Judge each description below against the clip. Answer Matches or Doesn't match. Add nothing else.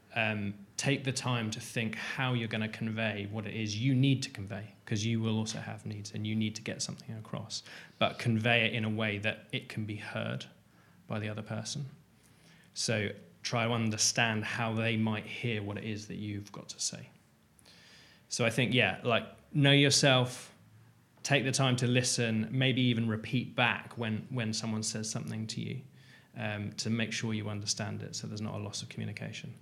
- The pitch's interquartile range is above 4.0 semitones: Doesn't match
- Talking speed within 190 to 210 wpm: Matches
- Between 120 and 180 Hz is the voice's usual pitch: Doesn't match